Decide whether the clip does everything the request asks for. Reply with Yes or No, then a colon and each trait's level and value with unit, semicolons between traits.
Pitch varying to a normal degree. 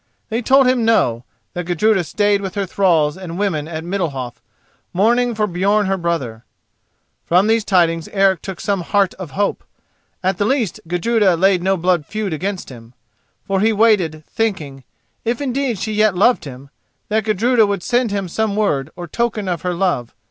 Yes: average, 4.1 semitones